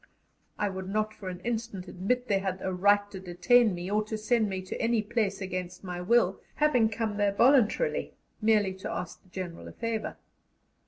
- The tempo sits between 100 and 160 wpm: No, average, 195 wpm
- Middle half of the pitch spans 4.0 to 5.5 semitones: No, average, 3.2 semitones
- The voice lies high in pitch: Yes, high, 205 Hz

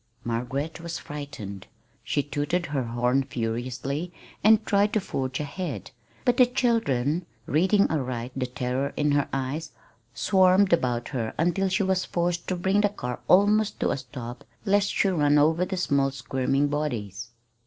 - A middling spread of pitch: No, wide, 6.4 semitones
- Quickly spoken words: No, average, 155 wpm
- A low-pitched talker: No, medium, 145 Hz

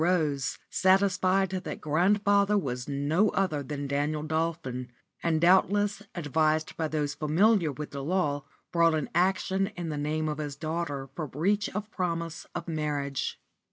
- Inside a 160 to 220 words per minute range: No, average, 150 wpm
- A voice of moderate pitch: Yes, medium, 160 Hz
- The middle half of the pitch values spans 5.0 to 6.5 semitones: No, average, 4.1 semitones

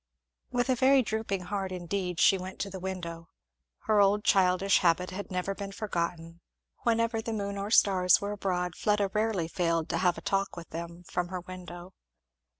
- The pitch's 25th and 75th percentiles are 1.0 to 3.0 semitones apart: Yes, narrow, 2.5 semitones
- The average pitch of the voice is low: No, high, 190 Hz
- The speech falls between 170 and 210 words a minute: Yes, average, 185 wpm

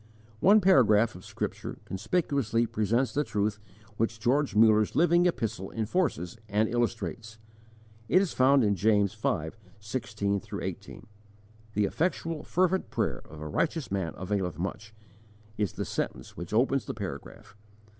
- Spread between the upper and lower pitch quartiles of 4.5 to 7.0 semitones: Yes, average, 5.1 semitones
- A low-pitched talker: Yes, low, 110 Hz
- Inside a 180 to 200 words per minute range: No, average, 140 wpm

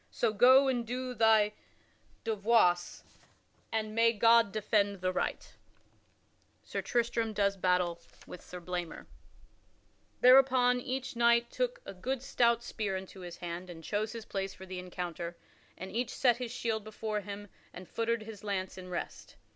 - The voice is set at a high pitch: Yes, high, 215 Hz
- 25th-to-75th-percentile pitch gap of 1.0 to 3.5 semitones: No, average, 4.1 semitones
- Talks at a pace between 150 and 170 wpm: Yes, average, 155 wpm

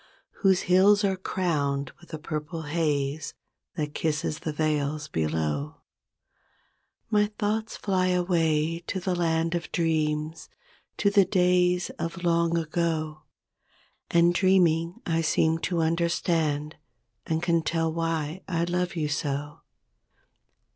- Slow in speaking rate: Yes, slow, 120 wpm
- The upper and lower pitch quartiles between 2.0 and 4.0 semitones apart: Yes, narrow, 2.6 semitones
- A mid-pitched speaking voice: Yes, medium, 165 Hz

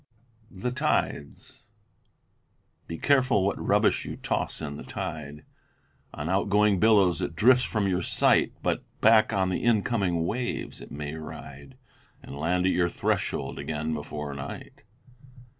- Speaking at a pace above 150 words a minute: No, average, 140 wpm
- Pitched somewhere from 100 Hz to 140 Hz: No, very low, 90 Hz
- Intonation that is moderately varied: No, wide, 5.9 semitones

